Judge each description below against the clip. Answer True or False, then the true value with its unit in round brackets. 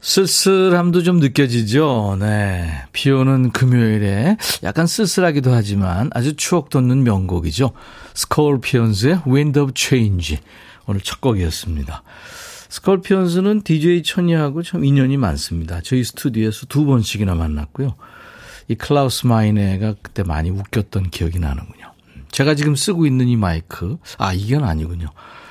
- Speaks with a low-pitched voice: True (125 Hz)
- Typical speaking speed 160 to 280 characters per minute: False (325 characters per minute)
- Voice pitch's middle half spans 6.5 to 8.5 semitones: True (7.2 semitones)